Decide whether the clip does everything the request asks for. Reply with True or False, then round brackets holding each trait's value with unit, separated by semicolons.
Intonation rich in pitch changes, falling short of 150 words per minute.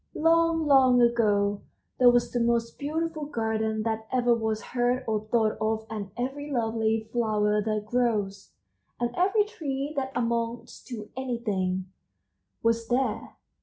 False (3.2 semitones; 135 wpm)